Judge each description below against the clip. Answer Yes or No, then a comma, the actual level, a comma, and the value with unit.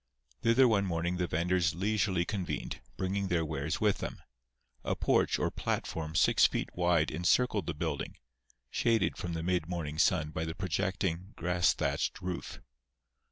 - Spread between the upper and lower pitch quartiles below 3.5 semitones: Yes, average, 2.7 semitones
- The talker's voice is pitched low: Yes, very low, 90 Hz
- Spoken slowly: No, average, 155 wpm